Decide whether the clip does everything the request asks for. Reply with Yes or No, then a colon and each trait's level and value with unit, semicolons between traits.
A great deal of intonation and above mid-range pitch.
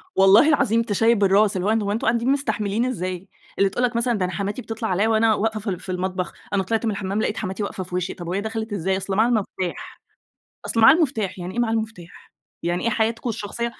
No: average, 3.2 semitones; high, 210 Hz